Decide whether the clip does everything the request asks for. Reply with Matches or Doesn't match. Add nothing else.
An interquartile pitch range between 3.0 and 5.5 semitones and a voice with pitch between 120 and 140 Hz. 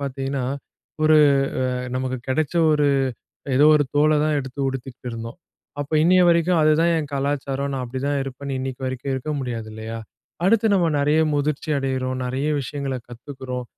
Doesn't match